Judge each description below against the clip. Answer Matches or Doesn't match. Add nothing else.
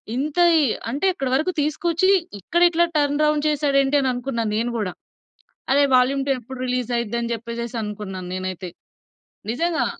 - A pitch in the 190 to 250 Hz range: Doesn't match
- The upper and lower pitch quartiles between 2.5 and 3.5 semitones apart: Doesn't match